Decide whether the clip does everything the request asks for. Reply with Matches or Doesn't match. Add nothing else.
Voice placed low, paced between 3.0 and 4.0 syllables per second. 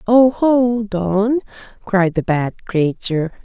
Doesn't match